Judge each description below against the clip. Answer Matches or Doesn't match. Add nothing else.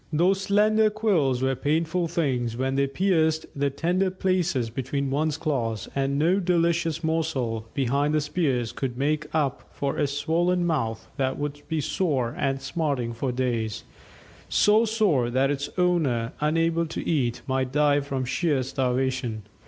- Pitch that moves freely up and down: Doesn't match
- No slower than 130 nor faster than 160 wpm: Matches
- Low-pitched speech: Doesn't match